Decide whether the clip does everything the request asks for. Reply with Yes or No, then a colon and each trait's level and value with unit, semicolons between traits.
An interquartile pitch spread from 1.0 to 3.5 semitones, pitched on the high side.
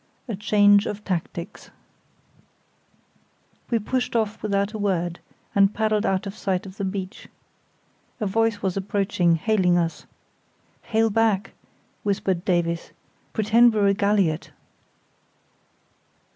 Yes: narrow, 2.4 semitones; high, 200 Hz